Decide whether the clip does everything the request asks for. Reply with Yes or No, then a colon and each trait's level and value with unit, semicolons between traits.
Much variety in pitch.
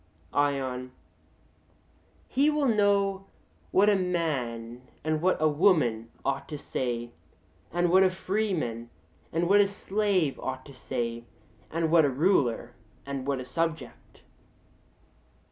Yes: wide, 6.9 semitones